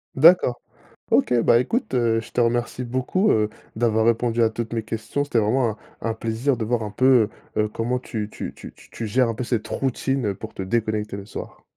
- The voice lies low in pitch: Yes, low, 115 Hz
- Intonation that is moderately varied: No, narrow, 2.3 semitones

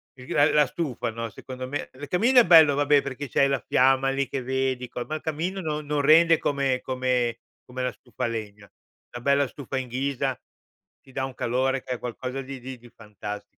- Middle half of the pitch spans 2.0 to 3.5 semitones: Yes, narrow, 2.4 semitones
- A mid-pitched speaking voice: No, low, 130 Hz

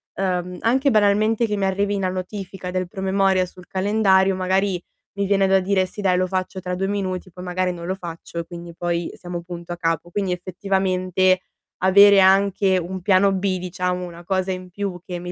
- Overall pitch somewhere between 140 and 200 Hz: Yes, medium, 185 Hz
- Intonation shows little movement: Yes, narrow, 1.4 semitones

